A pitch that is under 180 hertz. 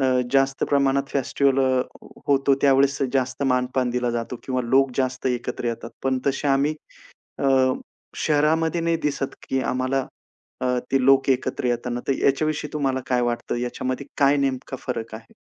Yes: low, 135 Hz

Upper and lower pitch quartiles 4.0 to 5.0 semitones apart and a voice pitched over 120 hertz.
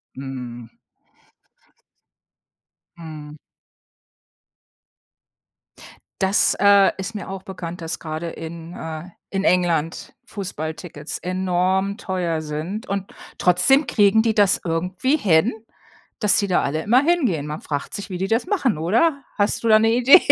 Yes: average, 4.5 semitones; medium, 185 Hz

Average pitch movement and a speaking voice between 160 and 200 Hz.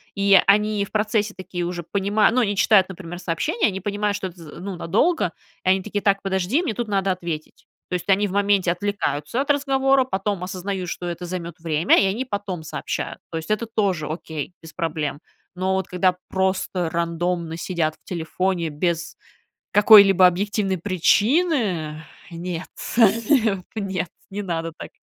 Yes: average, 3.2 semitones; high, 190 Hz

